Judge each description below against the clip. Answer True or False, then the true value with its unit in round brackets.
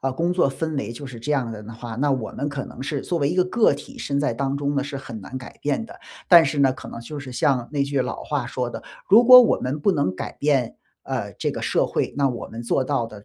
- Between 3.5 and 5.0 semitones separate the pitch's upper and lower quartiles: False (3.0 semitones)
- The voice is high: False (140 Hz)